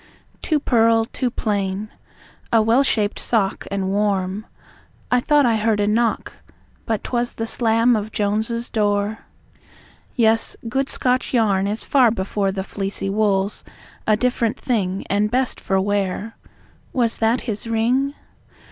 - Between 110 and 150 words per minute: Yes, average, 140 wpm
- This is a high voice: Yes, high, 220 Hz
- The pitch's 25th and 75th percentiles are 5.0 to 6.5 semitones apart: No, average, 2.7 semitones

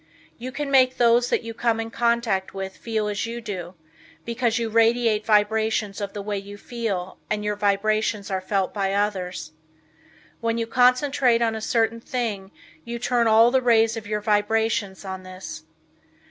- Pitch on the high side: Yes, high, 220 Hz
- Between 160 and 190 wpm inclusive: Yes, average, 175 wpm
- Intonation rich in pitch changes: No, narrow, 2.5 semitones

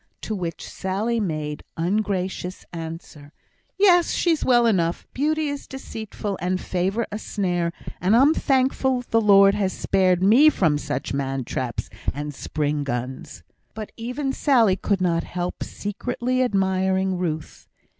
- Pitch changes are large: Yes, wide, 5.9 semitones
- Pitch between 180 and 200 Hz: Yes, high, 190 Hz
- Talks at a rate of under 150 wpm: Yes, slow, 135 wpm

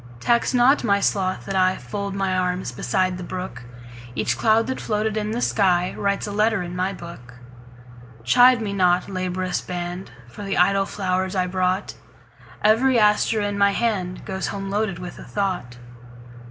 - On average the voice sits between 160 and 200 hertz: Yes, medium, 185 Hz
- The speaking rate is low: No, average, 145 wpm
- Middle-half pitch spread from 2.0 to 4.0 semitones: Yes, average, 2.7 semitones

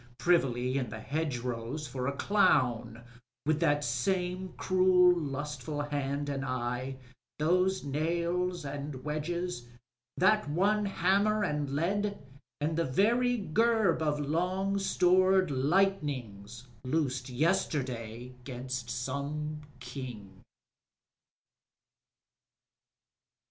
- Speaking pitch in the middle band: Yes, medium, 150 Hz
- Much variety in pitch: Yes, wide, 5.9 semitones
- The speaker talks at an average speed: No, slow, 95 wpm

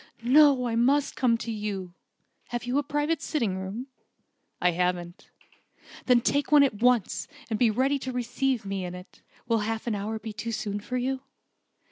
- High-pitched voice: Yes, high, 235 Hz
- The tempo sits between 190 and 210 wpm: No, average, 180 wpm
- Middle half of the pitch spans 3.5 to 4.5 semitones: Yes, average, 4.1 semitones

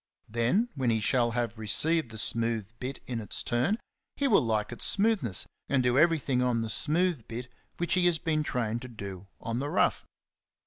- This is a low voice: Yes, low, 125 Hz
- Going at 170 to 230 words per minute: Yes, average, 190 wpm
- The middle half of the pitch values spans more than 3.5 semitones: Yes, average, 5.3 semitones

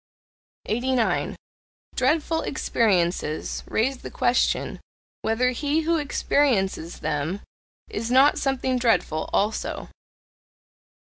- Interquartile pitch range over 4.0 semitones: Yes, average, 5.0 semitones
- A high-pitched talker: Yes, very high, 250 Hz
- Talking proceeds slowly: Yes, slow, 85 wpm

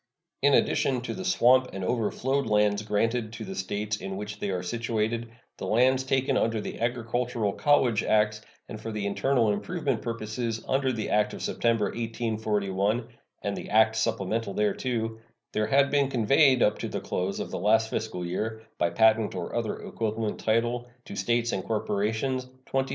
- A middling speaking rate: Yes, average, 170 wpm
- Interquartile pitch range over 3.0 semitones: No, narrow, 2.6 semitones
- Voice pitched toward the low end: Yes, low, 110 Hz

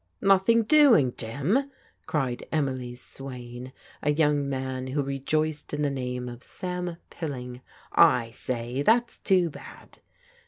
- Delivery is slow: Yes, slow, 130 wpm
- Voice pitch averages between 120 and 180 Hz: Yes, medium, 140 Hz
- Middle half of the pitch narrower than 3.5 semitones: No, average, 5.0 semitones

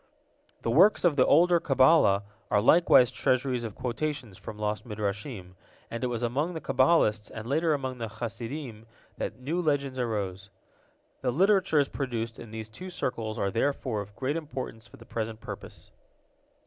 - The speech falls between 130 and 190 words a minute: Yes, average, 160 wpm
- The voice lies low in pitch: Yes, low, 125 Hz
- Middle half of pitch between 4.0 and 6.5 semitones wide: Yes, average, 4.8 semitones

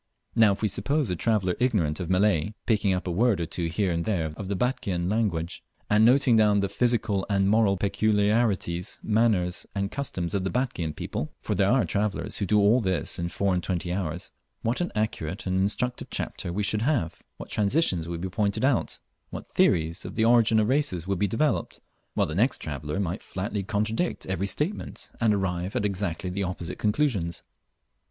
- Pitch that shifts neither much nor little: Yes, average, 3.8 semitones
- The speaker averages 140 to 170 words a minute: No, average, 190 wpm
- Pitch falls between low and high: No, low, 100 Hz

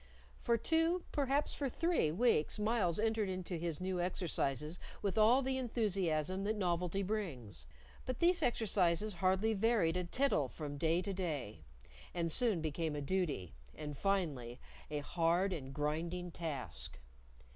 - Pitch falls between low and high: Yes, medium, 180 Hz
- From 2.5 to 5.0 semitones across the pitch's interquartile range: No, wide, 5.5 semitones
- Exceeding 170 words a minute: No, average, 145 wpm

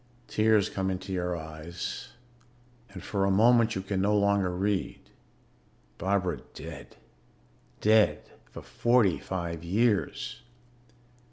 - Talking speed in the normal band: No, slow, 110 wpm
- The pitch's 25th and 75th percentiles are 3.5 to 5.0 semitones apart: No, average, 2.8 semitones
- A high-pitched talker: No, very low, 95 Hz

